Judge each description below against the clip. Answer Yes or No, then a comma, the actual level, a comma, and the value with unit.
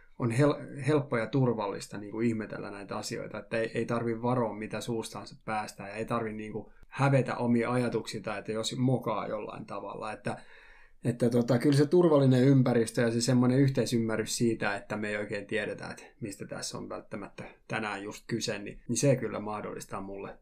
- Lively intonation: No, narrow, 2.6 semitones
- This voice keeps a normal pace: No, fast, 175 wpm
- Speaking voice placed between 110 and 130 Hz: Yes, low, 115 Hz